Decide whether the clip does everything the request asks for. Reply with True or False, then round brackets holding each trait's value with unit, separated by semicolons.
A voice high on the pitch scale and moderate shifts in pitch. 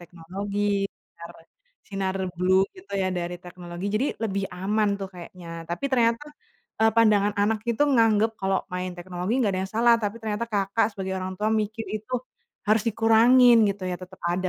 True (200 Hz; 3.2 semitones)